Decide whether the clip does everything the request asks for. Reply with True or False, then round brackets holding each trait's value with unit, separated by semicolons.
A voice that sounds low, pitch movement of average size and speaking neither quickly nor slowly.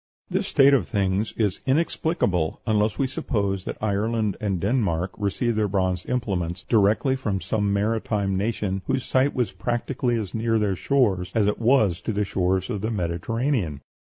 True (105 Hz; 3.7 semitones; 165 wpm)